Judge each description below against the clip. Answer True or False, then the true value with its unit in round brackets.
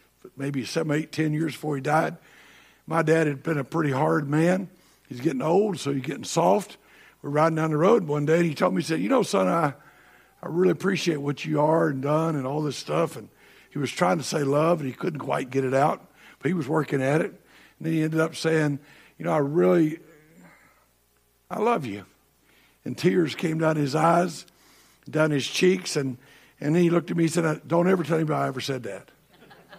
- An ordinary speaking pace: False (225 wpm)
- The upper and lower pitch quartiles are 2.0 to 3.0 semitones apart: True (2.7 semitones)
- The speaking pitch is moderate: True (155 Hz)